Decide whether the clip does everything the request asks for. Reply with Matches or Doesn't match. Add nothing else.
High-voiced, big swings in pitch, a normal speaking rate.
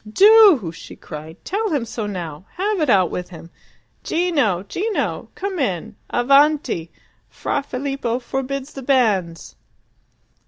Doesn't match